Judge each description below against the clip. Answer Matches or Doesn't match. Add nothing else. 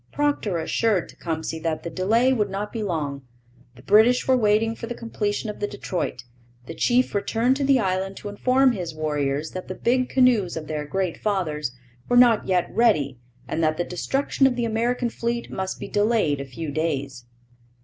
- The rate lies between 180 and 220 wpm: Matches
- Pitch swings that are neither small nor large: Doesn't match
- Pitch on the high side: Matches